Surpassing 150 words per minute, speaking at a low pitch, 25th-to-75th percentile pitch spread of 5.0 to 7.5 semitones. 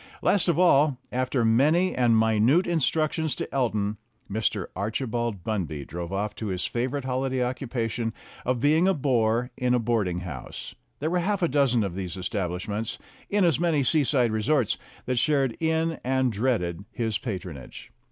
Yes: average, 160 wpm; low, 120 Hz; average, 5.3 semitones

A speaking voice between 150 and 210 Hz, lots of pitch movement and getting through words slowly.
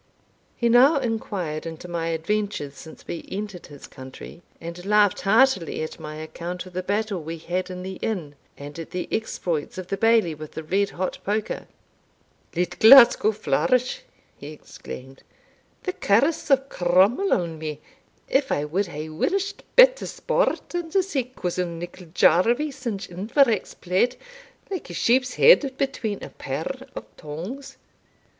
No: high, 190 Hz; wide, 6.9 semitones; average, 155 wpm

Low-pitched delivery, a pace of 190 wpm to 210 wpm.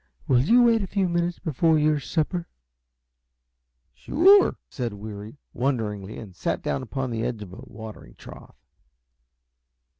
No: low, 130 Hz; average, 145 wpm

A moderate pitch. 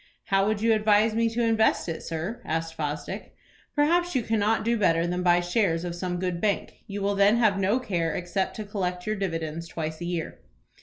No: high, 195 Hz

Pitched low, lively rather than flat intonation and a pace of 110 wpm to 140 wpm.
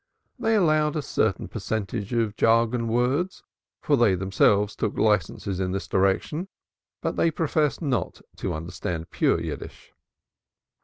Yes: low, 115 Hz; wide, 7.4 semitones; slow, 135 wpm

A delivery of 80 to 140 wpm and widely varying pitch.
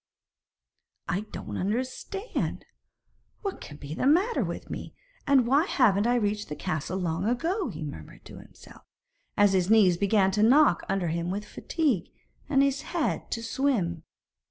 No: average, 155 wpm; wide, 7.2 semitones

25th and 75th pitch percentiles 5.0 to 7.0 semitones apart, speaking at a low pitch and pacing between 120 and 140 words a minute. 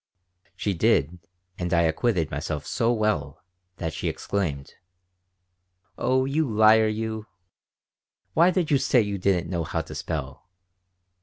Yes: wide, 5.5 semitones; low, 100 Hz; slow, 135 wpm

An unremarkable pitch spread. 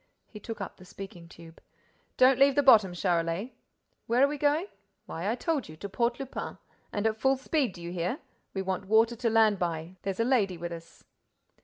No: wide, 6.3 semitones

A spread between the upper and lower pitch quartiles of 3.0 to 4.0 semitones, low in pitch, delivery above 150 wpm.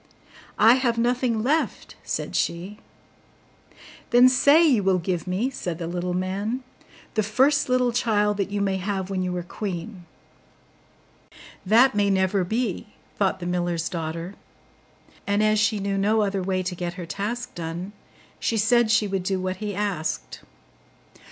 No: average, 3.5 semitones; high, 200 Hz; average, 160 wpm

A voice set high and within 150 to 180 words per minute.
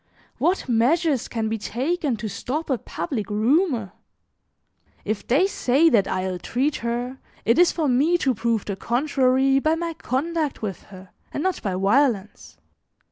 Yes: very high, 255 Hz; average, 160 wpm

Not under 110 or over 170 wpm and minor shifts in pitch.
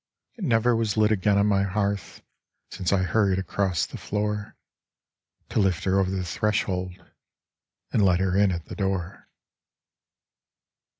Yes: average, 145 wpm; narrow, 2.1 semitones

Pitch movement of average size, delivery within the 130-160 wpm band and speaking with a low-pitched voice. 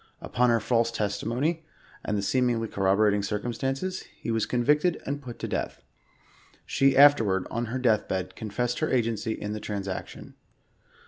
No: average, 3.8 semitones; average, 175 wpm; low, 115 Hz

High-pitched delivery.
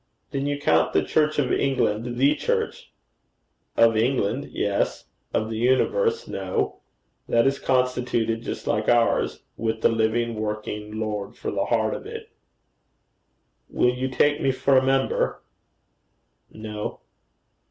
No: low, 120 Hz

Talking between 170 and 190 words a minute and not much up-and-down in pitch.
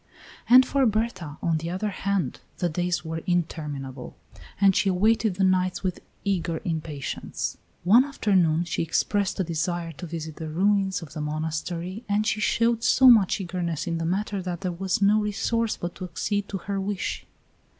No: average, 175 wpm; average, 3.7 semitones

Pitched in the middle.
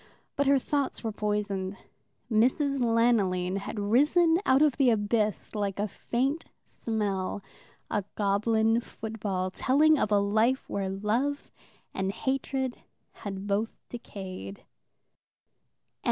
No: high, 220 Hz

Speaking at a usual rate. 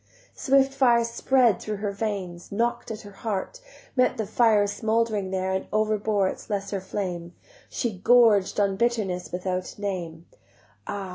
Yes: average, 150 wpm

